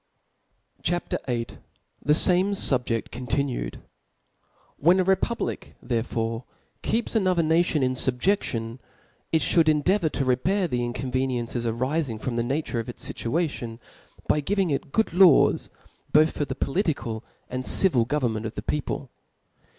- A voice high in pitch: No, low, 135 Hz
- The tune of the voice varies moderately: No, wide, 6.0 semitones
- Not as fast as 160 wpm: Yes, slow, 135 wpm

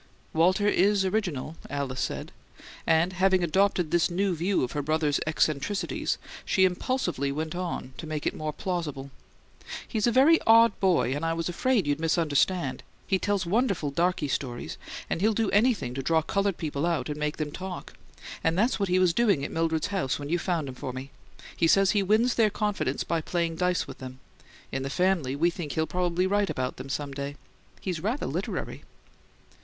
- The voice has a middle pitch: Yes, medium, 170 Hz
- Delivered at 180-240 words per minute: Yes, average, 190 wpm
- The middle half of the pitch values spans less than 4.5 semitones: No, average, 4.8 semitones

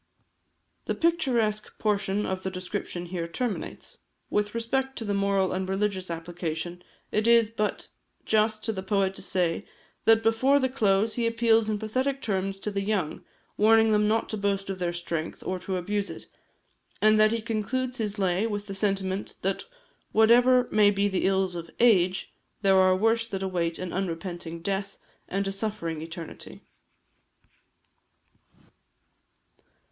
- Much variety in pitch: No, average, 3.0 semitones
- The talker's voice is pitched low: No, high, 200 Hz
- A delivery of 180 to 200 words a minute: No, average, 155 wpm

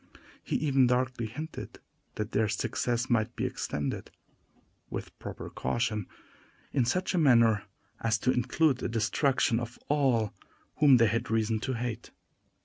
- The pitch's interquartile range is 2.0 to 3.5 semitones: Yes, average, 2.9 semitones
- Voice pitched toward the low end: Yes, low, 120 Hz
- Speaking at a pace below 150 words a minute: Yes, average, 140 wpm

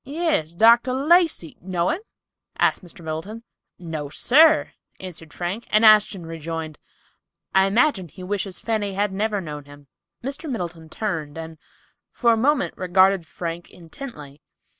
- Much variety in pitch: Yes, wide, 5.9 semitones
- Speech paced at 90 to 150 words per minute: Yes, average, 140 wpm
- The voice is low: No, high, 190 Hz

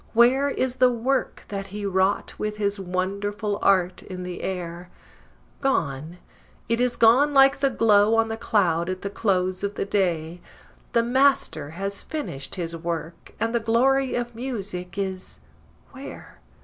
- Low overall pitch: No, high, 200 Hz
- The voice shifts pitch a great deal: No, average, 4.6 semitones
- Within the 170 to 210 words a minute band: No, average, 155 wpm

